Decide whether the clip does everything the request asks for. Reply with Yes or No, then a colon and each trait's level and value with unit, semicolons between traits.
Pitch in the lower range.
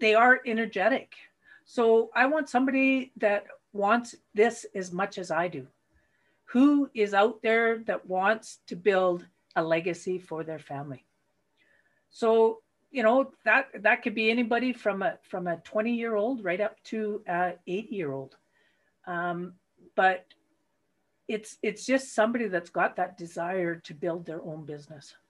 No: high, 210 Hz